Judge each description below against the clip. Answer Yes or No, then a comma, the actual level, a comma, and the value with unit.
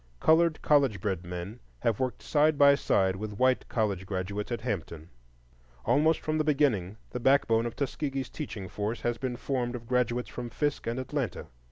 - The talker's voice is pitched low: Yes, low, 120 Hz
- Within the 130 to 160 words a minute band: No, average, 175 wpm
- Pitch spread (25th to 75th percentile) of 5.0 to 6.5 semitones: Yes, average, 5.3 semitones